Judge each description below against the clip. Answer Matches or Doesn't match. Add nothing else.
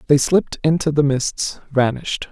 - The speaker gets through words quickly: Doesn't match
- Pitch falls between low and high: Matches